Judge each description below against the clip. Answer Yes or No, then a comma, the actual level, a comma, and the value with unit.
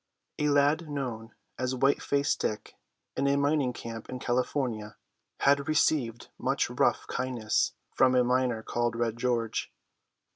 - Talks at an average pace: Yes, average, 145 wpm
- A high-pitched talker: No, low, 125 Hz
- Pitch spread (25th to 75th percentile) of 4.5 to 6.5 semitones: No, average, 3.3 semitones